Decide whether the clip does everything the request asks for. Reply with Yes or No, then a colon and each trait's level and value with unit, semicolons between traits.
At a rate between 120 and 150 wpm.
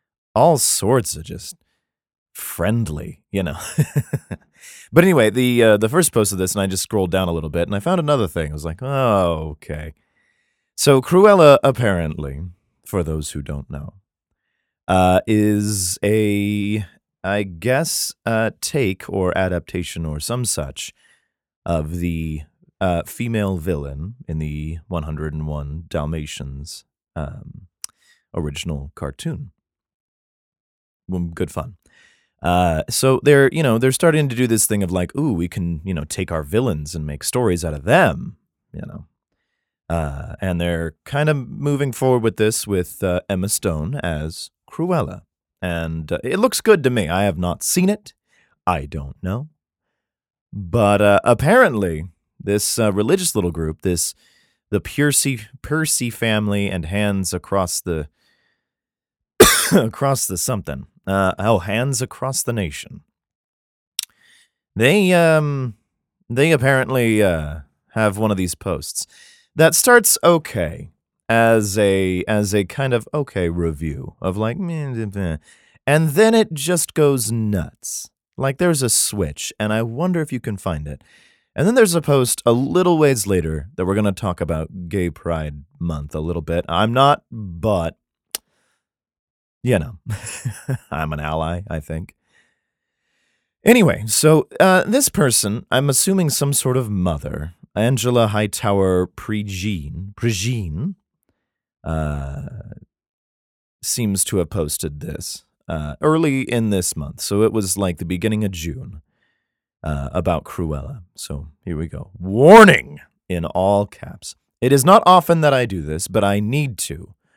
Yes: average, 145 wpm